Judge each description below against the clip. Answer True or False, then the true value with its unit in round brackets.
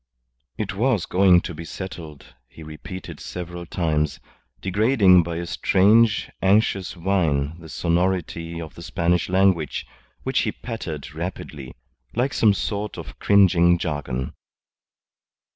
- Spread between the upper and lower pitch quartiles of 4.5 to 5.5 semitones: False (3.1 semitones)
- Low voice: True (90 Hz)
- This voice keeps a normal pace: False (125 wpm)